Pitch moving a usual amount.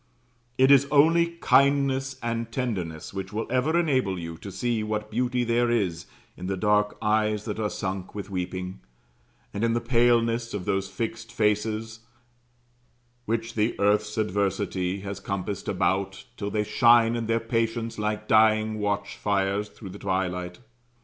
Yes: average, 3.0 semitones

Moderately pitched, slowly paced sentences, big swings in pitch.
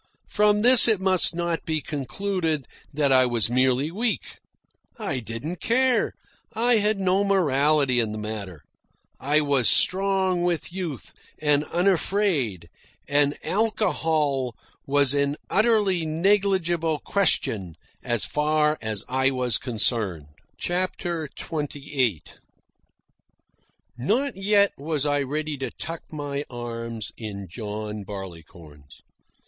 Yes: medium, 150 Hz; slow, 115 wpm; wide, 7.3 semitones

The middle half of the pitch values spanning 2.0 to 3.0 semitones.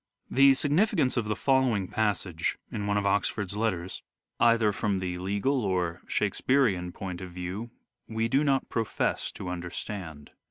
No: average, 4.5 semitones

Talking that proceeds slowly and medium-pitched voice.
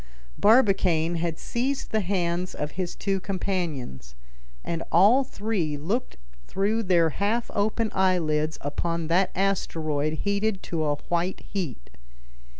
Yes: slow, 125 wpm; medium, 180 Hz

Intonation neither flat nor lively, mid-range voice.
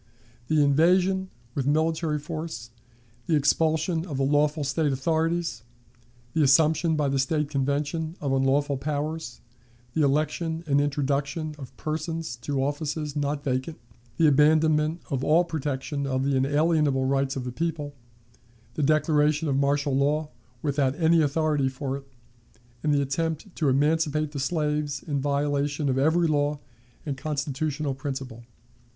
No: narrow, 2.2 semitones; medium, 145 Hz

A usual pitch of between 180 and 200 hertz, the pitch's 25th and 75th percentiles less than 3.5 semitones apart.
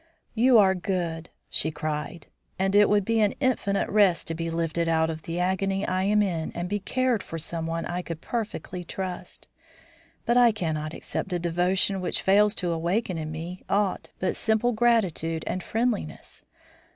No: medium, 185 Hz; average, 3.9 semitones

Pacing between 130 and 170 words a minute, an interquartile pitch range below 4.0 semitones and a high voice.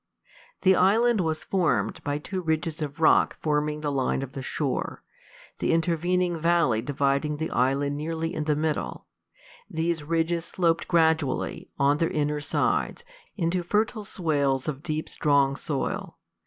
No: average, 145 wpm; average, 2.8 semitones; medium, 155 Hz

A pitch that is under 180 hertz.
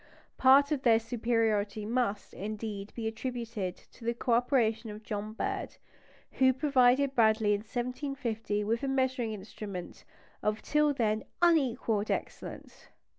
No: high, 230 Hz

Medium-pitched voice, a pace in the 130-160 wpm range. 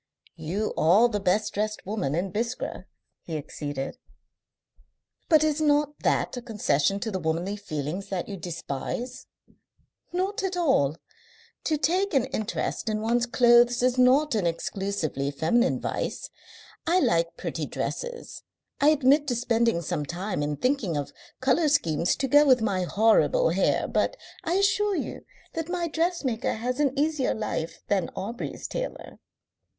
No: high, 230 Hz; average, 150 wpm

